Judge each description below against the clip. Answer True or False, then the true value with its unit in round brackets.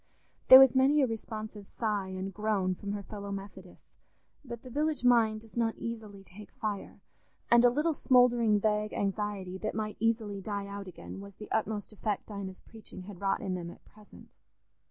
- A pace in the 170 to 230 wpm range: True (180 wpm)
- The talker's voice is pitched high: True (210 Hz)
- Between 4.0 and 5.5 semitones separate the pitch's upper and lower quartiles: False (2.5 semitones)